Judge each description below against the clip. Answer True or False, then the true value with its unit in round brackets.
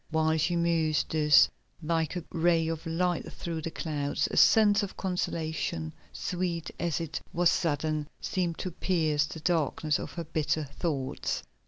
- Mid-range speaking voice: True (160 Hz)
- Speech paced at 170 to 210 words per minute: False (155 wpm)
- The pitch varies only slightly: True (2.0 semitones)